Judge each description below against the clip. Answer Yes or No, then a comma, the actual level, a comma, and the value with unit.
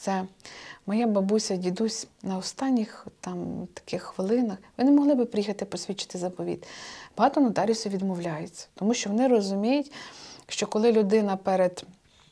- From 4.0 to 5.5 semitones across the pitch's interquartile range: No, average, 3.6 semitones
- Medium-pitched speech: No, high, 210 Hz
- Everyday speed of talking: Yes, average, 130 wpm